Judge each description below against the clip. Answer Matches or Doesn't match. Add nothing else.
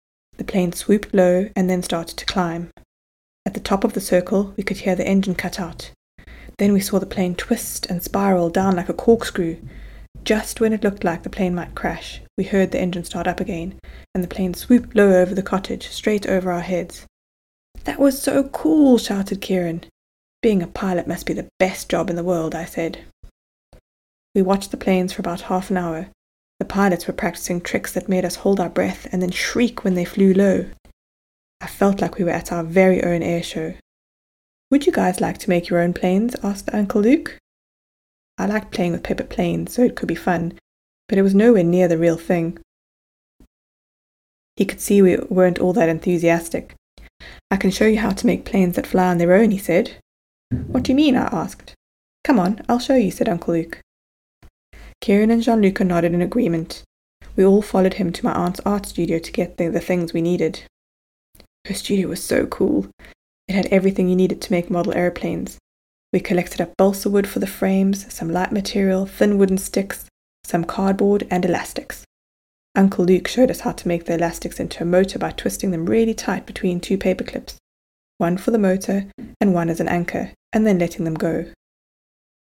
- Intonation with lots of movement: Doesn't match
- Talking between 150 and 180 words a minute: Doesn't match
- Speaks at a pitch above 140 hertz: Matches